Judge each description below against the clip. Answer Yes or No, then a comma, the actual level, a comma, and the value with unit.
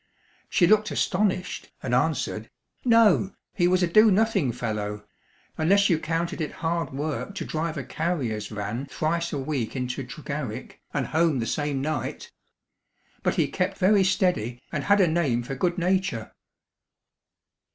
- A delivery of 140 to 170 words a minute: Yes, average, 150 wpm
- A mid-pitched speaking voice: Yes, medium, 155 Hz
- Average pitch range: No, wide, 5.9 semitones